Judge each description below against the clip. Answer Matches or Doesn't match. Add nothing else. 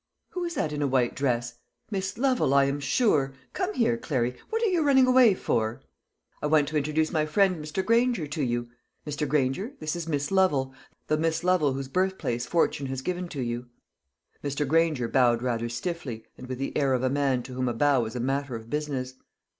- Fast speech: Matches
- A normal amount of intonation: Doesn't match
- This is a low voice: Doesn't match